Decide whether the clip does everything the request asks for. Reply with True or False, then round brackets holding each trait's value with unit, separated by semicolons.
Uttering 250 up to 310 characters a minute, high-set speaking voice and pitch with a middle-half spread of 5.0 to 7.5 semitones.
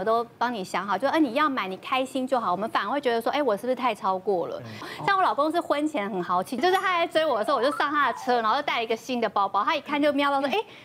False (415 characters per minute; 260 Hz; 5.3 semitones)